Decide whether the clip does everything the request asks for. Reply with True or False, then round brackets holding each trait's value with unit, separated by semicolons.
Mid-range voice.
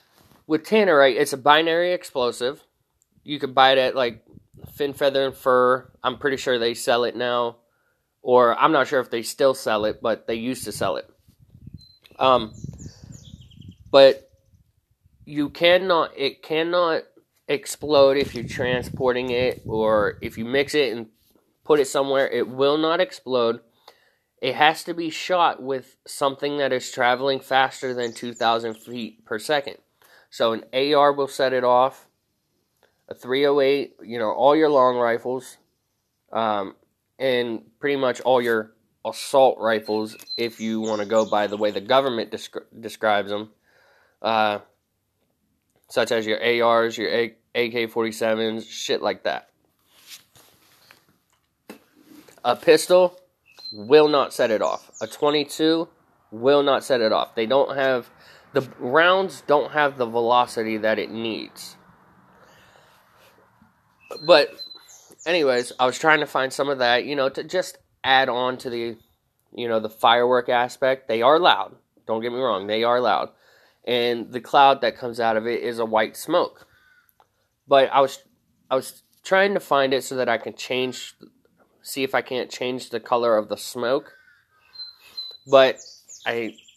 False (125 Hz)